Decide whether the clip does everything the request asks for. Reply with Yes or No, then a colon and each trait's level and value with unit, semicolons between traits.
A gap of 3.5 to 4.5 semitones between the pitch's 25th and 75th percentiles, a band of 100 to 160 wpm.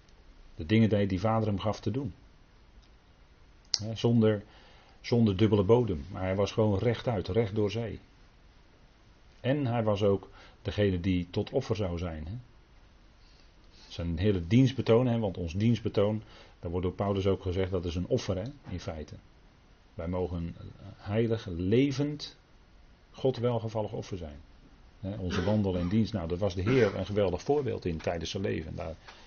Yes: average, 3.9 semitones; average, 155 wpm